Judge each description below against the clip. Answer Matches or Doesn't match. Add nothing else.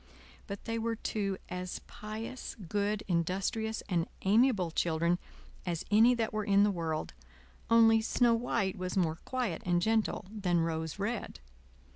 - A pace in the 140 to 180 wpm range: Matches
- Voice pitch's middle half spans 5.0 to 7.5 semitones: Doesn't match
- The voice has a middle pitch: Doesn't match